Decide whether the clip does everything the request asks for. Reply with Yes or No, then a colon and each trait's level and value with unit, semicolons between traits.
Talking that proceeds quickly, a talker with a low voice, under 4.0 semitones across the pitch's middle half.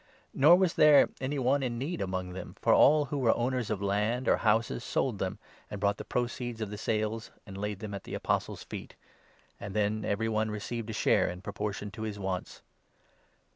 Yes: fast, 210 wpm; low, 110 Hz; average, 3.2 semitones